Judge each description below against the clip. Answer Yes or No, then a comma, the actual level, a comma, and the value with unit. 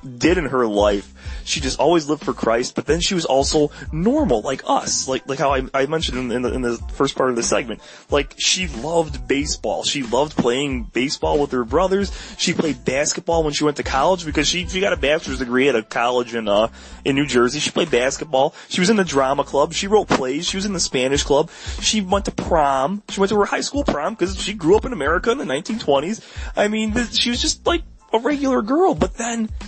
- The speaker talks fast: Yes, fast, 240 wpm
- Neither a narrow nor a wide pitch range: No, wide, 7.6 semitones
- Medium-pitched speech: Yes, medium, 165 Hz